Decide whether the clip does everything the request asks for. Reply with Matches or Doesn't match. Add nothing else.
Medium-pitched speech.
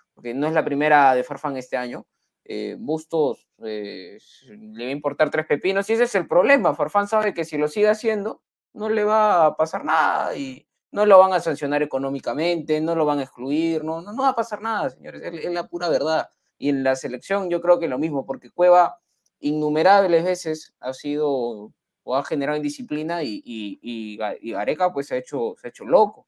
Matches